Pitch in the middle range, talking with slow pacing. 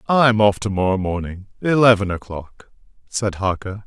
No: low, 105 Hz; slow, 110 wpm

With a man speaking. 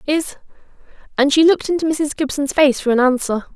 No: female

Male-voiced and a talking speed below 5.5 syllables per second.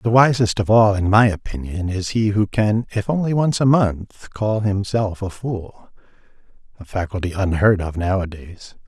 Yes: male; 4.5 syllables/s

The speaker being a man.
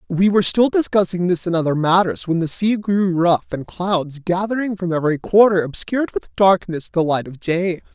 Yes: male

